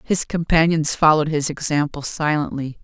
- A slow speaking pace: Yes, slow, 125 wpm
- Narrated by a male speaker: No, female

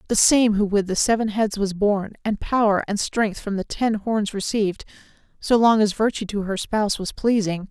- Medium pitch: No, high, 210 Hz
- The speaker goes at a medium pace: No, fast, 210 wpm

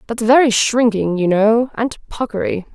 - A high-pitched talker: Yes, high, 230 Hz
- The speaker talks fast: No, average, 155 wpm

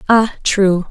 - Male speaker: No, female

